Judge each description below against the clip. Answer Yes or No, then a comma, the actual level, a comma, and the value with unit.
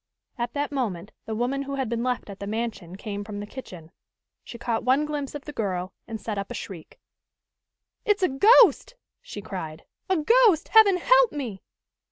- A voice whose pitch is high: Yes, high, 240 Hz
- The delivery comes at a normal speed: Yes, average, 190 wpm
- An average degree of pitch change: No, wide, 6.6 semitones